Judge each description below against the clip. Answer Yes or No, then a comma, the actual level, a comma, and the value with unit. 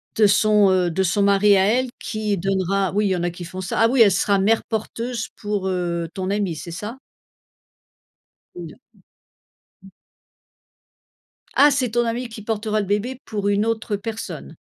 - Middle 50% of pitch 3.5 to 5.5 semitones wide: No, average, 2.8 semitones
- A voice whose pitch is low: No, high, 205 Hz